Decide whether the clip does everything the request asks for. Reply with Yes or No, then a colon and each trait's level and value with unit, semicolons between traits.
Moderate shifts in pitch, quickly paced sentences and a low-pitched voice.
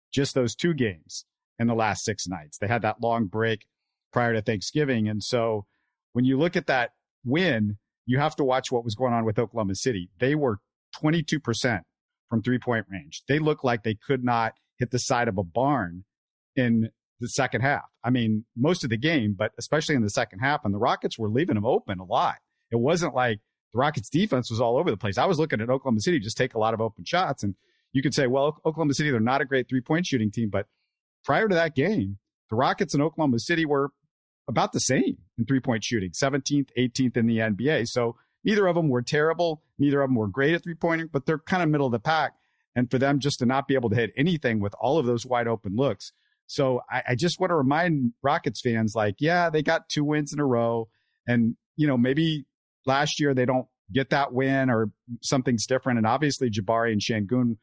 Yes: average, 4.1 semitones; fast, 230 wpm; low, 125 Hz